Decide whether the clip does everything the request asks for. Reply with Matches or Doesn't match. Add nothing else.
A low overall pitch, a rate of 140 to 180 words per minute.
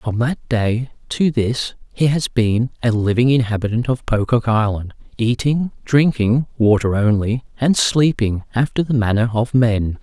Matches